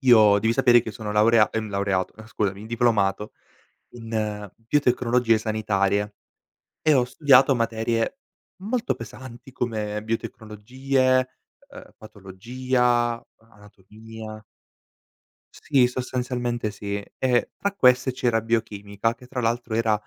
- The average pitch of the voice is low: Yes, low, 115 Hz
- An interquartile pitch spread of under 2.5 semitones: No, average, 2.8 semitones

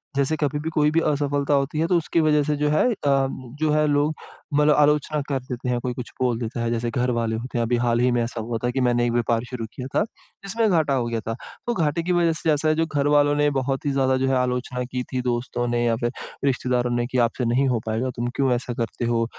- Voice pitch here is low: Yes, low, 130 Hz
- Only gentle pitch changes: No, average, 3.5 semitones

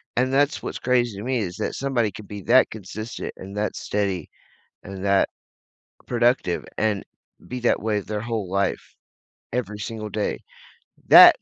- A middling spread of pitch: Yes, average, 3.4 semitones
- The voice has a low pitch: Yes, low, 110 Hz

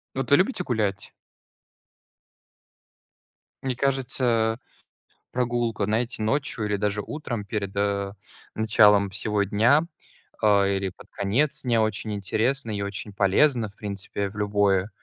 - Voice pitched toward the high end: No, low, 105 Hz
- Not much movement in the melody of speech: No, average, 3.3 semitones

